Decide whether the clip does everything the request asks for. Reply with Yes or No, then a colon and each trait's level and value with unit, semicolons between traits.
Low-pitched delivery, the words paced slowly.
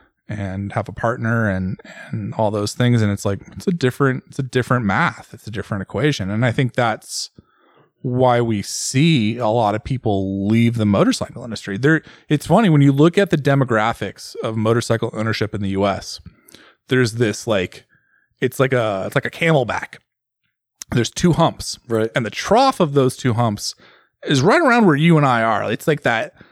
No: low, 115 Hz; average, 190 wpm